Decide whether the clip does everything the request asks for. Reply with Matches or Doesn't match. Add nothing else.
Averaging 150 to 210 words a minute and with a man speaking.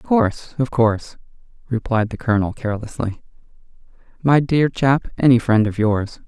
Doesn't match